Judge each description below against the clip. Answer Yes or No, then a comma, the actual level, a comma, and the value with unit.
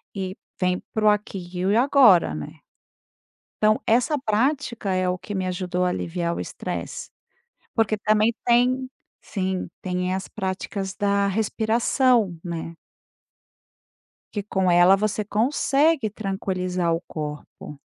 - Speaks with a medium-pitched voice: No, high, 195 Hz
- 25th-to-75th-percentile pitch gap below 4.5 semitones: Yes, average, 3.3 semitones